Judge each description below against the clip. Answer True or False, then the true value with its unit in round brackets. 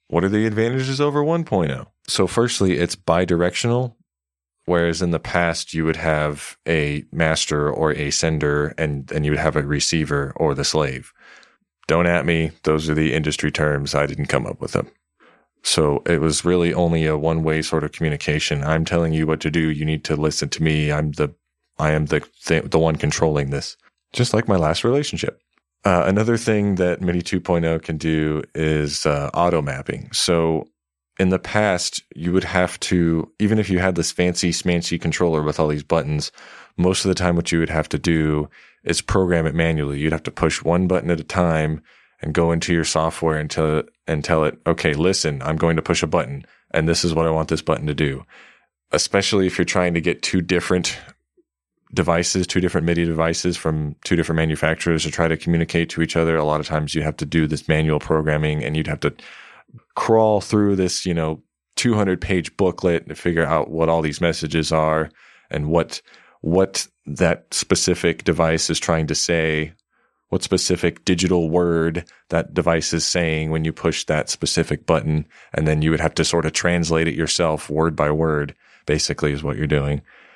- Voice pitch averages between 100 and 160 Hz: False (80 Hz)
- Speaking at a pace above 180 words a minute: True (195 wpm)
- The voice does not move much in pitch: True (2.2 semitones)